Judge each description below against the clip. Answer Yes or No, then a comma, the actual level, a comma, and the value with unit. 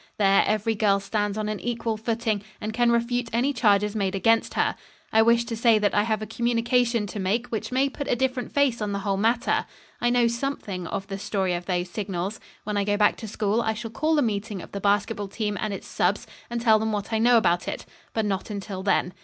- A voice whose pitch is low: No, high, 215 Hz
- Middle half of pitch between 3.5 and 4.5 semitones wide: No, average, 2.7 semitones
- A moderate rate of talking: No, fast, 235 wpm